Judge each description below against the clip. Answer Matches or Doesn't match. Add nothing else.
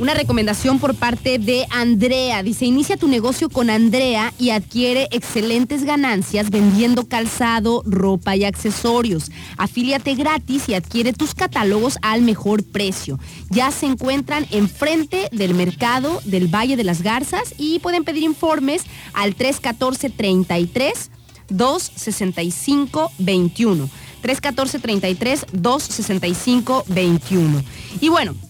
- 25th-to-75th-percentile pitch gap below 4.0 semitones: Doesn't match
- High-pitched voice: Matches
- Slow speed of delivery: Matches